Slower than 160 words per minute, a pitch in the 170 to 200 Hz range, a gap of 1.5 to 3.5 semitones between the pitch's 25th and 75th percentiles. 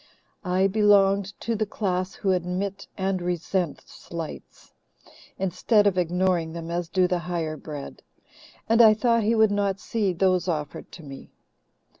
Yes: average, 150 wpm; medium, 185 Hz; average, 2.7 semitones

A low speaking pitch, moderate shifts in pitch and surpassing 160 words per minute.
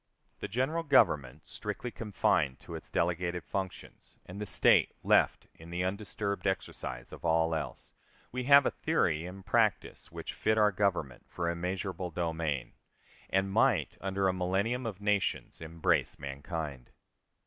No: very low, 95 Hz; average, 4.0 semitones; average, 145 wpm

